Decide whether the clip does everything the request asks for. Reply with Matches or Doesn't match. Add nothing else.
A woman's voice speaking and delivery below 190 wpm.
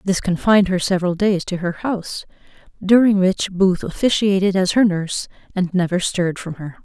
Matches